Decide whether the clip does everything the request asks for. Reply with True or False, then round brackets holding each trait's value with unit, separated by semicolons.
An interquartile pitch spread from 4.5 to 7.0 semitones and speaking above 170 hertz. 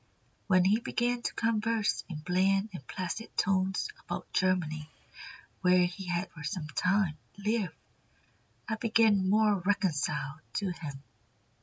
False (3.3 semitones; 185 Hz)